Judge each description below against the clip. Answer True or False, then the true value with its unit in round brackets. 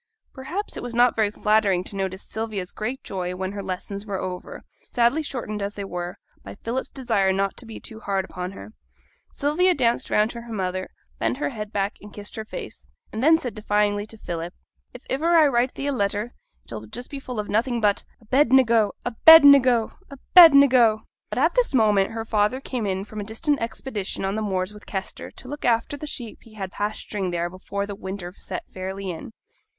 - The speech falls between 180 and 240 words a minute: True (205 wpm)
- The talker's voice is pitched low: False (215 Hz)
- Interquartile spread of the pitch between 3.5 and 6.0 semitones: True (4.2 semitones)